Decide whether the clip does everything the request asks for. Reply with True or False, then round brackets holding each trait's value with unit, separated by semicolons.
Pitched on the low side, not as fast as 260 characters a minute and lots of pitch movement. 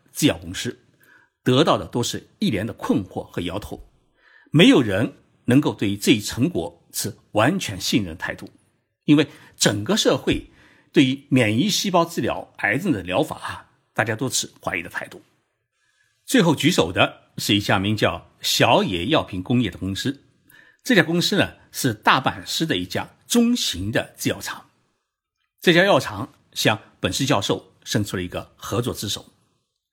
True (125 Hz; 240 characters per minute; 7.2 semitones)